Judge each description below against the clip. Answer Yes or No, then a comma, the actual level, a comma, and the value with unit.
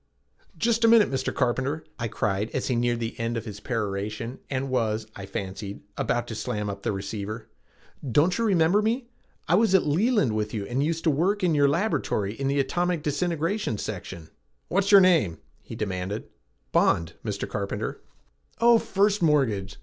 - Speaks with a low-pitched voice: Yes, low, 130 Hz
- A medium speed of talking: Yes, average, 175 wpm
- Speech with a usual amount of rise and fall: No, wide, 8.9 semitones